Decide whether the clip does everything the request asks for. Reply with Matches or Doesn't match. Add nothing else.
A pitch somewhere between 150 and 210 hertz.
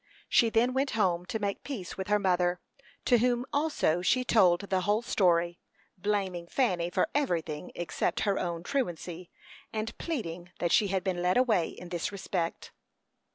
Matches